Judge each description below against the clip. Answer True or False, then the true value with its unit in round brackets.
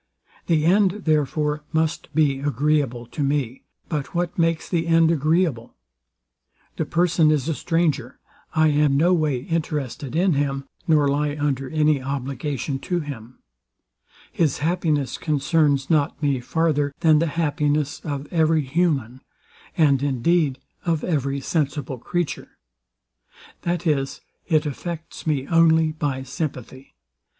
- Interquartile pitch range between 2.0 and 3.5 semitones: True (2.9 semitones)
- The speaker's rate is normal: False (130 wpm)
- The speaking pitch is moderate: True (150 Hz)